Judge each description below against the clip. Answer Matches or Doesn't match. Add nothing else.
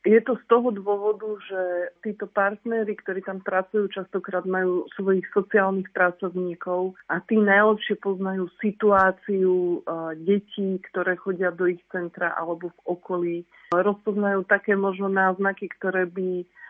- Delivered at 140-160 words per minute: Doesn't match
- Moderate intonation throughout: Doesn't match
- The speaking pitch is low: Doesn't match